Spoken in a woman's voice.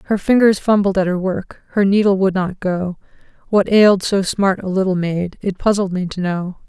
Yes: female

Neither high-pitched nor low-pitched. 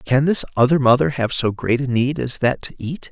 No: low, 130 Hz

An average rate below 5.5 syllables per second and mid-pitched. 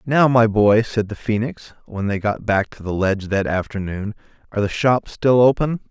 No: 5.0 syllables/s; low, 110 Hz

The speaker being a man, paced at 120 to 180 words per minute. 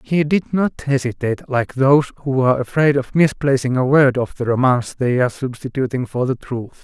No: male; average, 195 wpm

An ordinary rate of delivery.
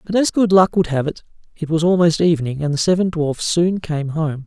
No: fast, 240 wpm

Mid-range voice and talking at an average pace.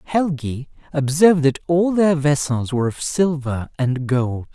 Yes: medium, 145 Hz; average, 145 wpm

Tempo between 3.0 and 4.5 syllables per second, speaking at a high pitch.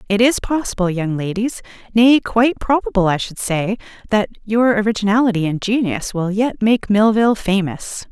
No: 5.1 syllables/s; high, 210 Hz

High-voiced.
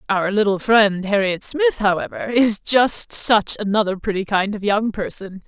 Yes: high, 205 Hz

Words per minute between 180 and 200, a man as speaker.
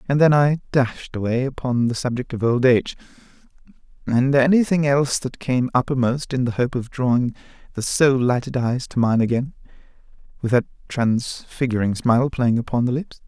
No: average, 170 wpm; male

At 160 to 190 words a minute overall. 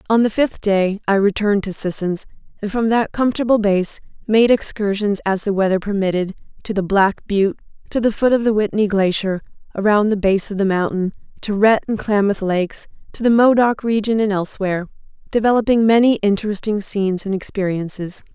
Yes: average, 175 wpm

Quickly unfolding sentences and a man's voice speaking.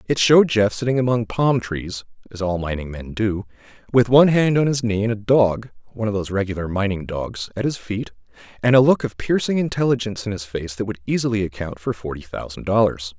Yes: fast, 215 wpm; male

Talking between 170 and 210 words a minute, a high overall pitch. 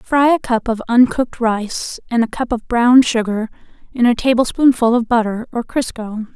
Yes: average, 180 wpm; high, 235 Hz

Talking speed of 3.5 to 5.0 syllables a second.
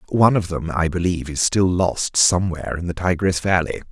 No: 5.8 syllables/s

